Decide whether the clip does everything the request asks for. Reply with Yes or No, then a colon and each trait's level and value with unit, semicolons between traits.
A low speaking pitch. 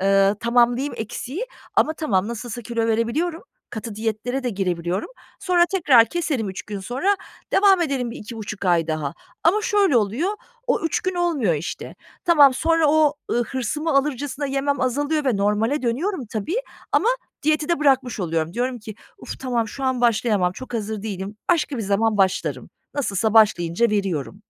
No: high, 240 Hz